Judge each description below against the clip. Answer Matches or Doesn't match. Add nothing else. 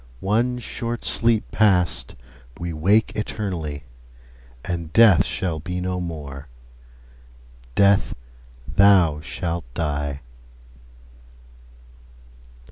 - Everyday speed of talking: Doesn't match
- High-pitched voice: Doesn't match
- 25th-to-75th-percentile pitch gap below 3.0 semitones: Doesn't match